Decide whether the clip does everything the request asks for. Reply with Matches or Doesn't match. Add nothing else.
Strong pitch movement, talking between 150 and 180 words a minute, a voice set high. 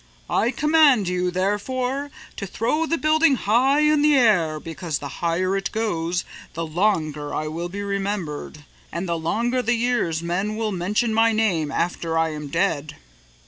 Matches